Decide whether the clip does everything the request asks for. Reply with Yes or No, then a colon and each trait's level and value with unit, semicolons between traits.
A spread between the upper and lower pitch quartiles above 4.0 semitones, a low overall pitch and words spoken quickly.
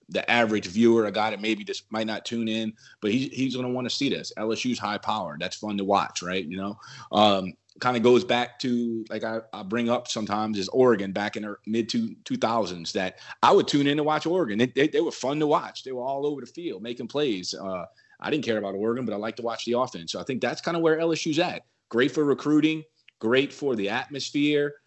Yes: average, 4.7 semitones; low, 120 Hz; fast, 250 wpm